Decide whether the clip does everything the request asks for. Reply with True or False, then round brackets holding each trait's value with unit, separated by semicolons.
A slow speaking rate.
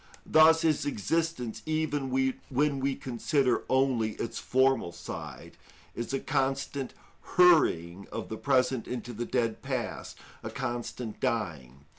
True (125 wpm)